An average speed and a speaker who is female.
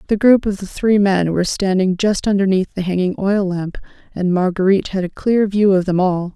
No: fast, 215 wpm; female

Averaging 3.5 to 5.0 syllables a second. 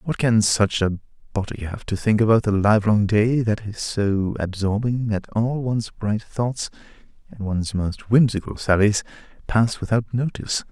Yes: 4.7 syllables/s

